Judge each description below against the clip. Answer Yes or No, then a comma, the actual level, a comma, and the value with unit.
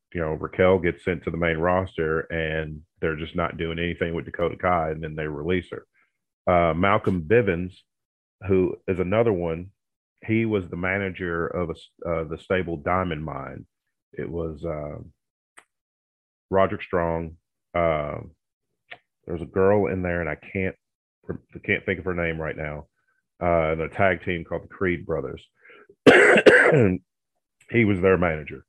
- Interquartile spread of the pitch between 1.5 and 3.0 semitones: Yes, narrow, 2.6 semitones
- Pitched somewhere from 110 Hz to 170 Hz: No, very low, 85 Hz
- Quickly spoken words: No, average, 160 wpm